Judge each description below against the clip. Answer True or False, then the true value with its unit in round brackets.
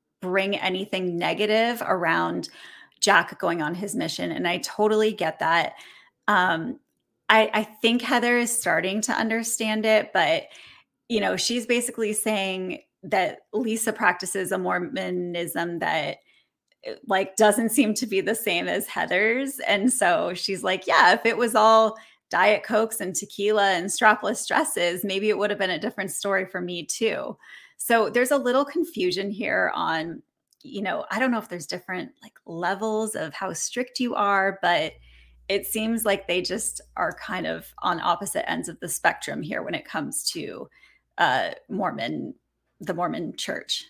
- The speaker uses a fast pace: False (165 wpm)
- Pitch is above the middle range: True (215 Hz)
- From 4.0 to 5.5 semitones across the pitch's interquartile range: False (3.3 semitones)